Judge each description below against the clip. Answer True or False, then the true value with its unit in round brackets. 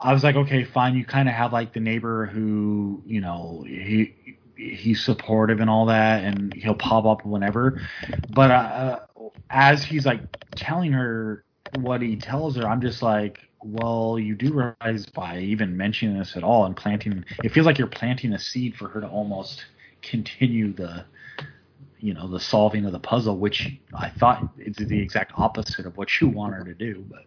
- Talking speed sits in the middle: True (190 wpm)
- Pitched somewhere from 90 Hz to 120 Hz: True (110 Hz)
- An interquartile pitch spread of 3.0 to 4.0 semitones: True (3.3 semitones)